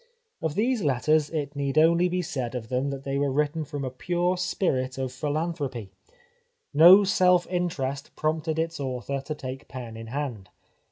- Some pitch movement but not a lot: Yes, average, 4.0 semitones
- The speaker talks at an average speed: Yes, average, 170 wpm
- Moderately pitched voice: Yes, medium, 145 Hz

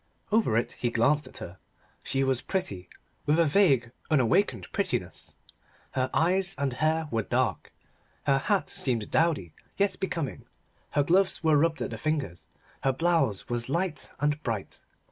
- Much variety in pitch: Yes, wide, 5.9 semitones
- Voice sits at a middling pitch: Yes, medium, 145 Hz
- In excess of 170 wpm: No, average, 155 wpm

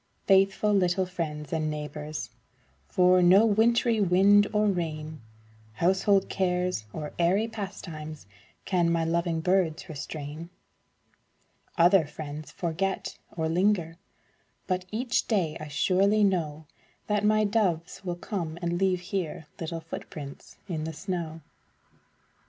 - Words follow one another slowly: Yes, slow, 120 wpm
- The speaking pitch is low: No, medium, 175 Hz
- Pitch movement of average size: Yes, average, 3.5 semitones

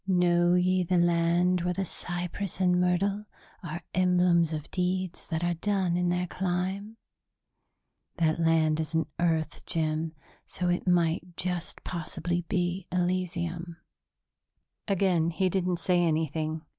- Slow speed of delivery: Yes, slow, 130 wpm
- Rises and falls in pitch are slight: Yes, narrow, 1.5 semitones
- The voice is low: No, medium, 175 Hz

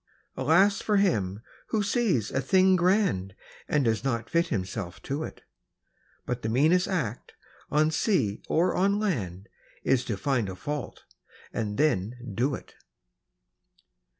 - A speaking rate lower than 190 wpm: Yes, average, 140 wpm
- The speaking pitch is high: No, low, 135 Hz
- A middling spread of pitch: No, wide, 8.8 semitones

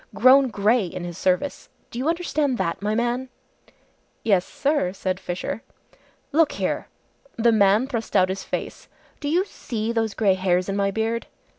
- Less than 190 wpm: Yes, average, 165 wpm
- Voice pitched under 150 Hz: No, high, 220 Hz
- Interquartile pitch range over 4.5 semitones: Yes, average, 5.2 semitones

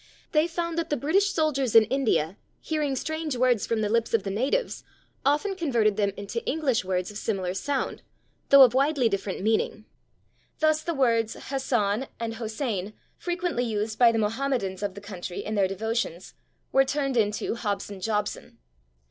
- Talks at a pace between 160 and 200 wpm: Yes, average, 165 wpm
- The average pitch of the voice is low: No, high, 230 Hz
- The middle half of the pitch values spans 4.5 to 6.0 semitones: Yes, average, 5.1 semitones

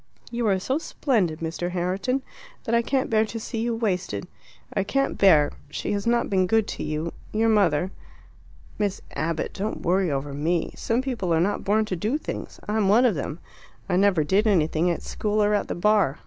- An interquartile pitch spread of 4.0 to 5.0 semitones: Yes, average, 4.5 semitones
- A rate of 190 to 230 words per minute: Yes, average, 200 wpm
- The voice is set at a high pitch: Yes, high, 200 Hz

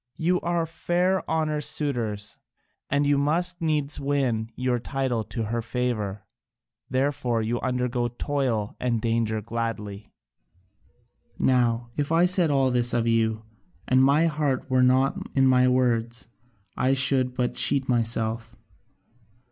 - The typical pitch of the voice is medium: No, low, 125 Hz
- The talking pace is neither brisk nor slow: No, slow, 130 wpm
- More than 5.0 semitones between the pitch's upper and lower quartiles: No, average, 3.6 semitones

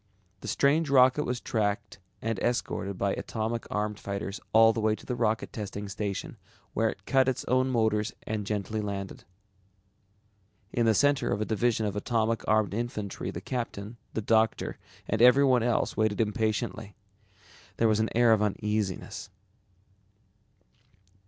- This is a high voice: No, low, 110 Hz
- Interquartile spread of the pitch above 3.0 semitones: No, narrow, 2.5 semitones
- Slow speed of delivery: No, average, 150 wpm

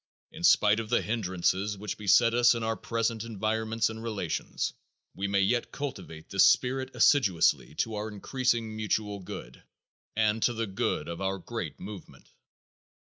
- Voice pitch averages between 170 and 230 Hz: No, low, 110 Hz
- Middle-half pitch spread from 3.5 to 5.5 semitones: No, average, 2.8 semitones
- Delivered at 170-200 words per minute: No, average, 155 wpm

